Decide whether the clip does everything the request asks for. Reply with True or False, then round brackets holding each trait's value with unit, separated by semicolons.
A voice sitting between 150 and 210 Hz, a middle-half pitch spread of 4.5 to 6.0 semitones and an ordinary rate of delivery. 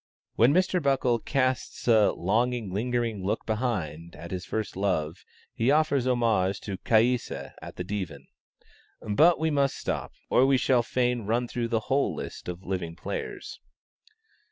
False (115 Hz; 5.0 semitones; 155 wpm)